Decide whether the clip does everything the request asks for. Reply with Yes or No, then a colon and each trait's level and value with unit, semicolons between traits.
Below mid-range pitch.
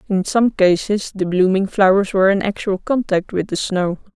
No: high, 195 Hz